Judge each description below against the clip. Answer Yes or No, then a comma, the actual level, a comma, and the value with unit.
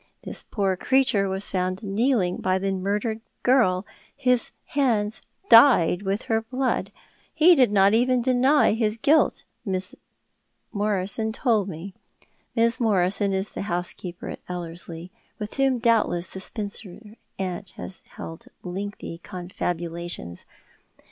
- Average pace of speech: No, slow, 125 wpm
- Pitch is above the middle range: Yes, high, 205 Hz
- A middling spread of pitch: Yes, average, 4.0 semitones